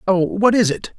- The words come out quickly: Yes, fast, 245 wpm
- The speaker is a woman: No, male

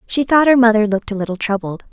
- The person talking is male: No, female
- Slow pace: No, fast, 250 wpm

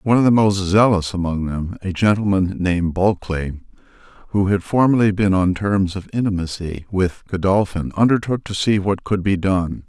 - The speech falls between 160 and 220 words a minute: Yes, average, 170 wpm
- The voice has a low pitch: Yes, very low, 95 Hz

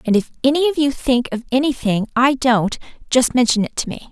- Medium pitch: No, very high, 255 Hz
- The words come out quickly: Yes, fast, 220 wpm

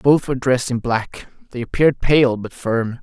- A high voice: No, low, 125 Hz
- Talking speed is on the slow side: No, average, 200 wpm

